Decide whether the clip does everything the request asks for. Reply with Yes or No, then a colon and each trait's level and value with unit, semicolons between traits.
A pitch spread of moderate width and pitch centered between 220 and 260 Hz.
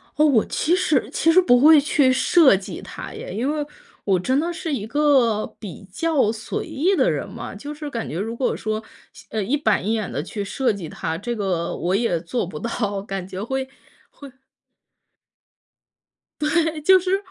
No: wide, 6.9 semitones; high, 245 Hz